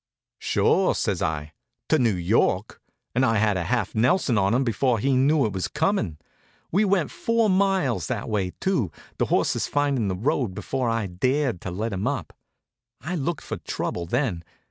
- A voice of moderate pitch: No, low, 120 Hz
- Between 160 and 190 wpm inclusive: Yes, average, 175 wpm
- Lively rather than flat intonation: Yes, wide, 7.2 semitones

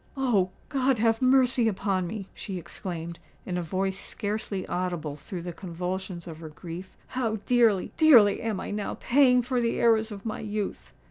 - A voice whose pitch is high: Yes, high, 200 Hz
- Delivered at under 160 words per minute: No, average, 170 wpm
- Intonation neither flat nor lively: Yes, average, 4.4 semitones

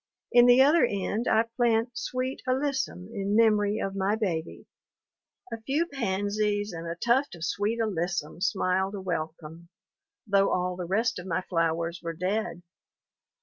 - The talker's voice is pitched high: Yes, high, 200 Hz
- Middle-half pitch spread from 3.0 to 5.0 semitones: Yes, average, 4.4 semitones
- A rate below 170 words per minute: Yes, average, 150 wpm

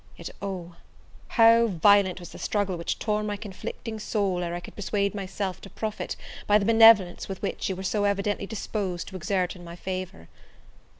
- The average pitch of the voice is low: No, high, 195 Hz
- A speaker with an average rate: Yes, average, 180 wpm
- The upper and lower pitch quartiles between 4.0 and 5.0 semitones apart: No, narrow, 2.4 semitones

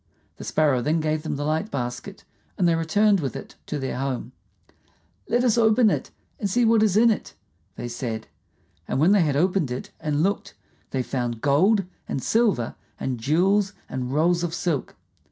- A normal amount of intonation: No, wide, 7.1 semitones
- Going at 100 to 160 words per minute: No, average, 180 wpm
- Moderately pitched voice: Yes, medium, 160 Hz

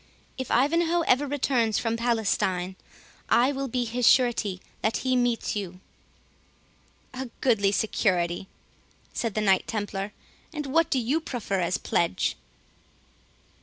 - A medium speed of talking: No, slow, 130 wpm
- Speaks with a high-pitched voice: Yes, high, 230 Hz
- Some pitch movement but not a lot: Yes, average, 4.8 semitones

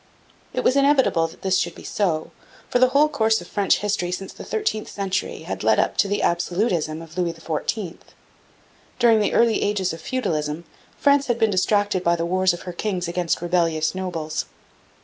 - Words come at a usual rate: Yes, average, 190 wpm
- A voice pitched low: No, medium, 185 Hz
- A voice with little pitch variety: No, average, 4.3 semitones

